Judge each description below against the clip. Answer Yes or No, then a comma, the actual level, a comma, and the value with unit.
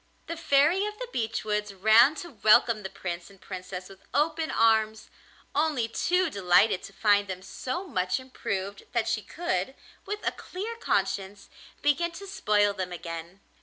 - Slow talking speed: No, average, 165 wpm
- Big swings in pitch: Yes, wide, 8.2 semitones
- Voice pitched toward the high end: Yes, high, 220 Hz